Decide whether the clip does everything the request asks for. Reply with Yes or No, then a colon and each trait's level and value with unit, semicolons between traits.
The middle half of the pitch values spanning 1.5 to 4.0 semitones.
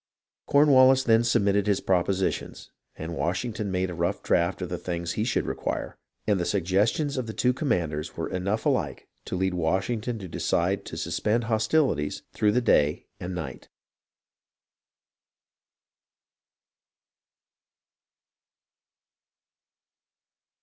No: average, 4.7 semitones